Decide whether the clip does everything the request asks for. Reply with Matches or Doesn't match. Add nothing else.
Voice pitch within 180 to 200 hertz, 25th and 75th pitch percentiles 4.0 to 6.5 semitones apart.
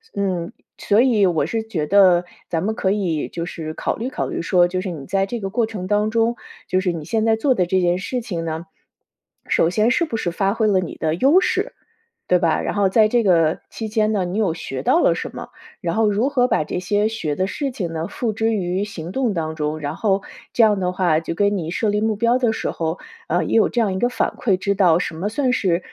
Matches